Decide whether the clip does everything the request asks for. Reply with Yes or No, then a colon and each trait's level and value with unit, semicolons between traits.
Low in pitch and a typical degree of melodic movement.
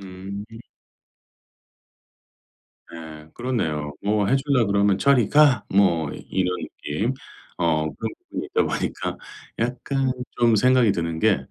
No: low, 100 Hz; wide, 6.8 semitones